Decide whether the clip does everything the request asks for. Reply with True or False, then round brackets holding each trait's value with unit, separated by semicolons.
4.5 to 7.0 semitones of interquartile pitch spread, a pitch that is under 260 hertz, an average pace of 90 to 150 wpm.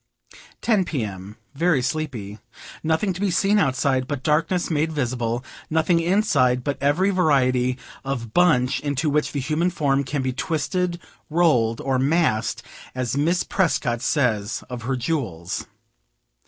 True (4.8 semitones; 140 Hz; 140 wpm)